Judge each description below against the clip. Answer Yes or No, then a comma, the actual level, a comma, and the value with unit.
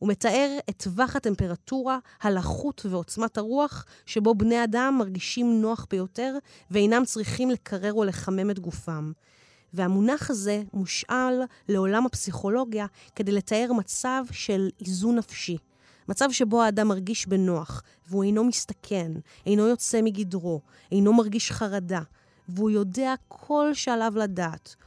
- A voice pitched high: Yes, high, 215 Hz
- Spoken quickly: No, average, 125 wpm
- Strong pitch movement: No, average, 3.9 semitones